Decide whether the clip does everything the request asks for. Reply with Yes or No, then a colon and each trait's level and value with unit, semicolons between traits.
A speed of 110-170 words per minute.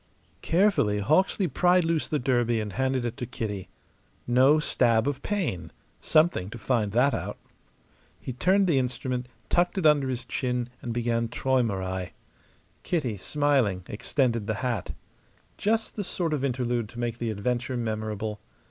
Yes: average, 150 wpm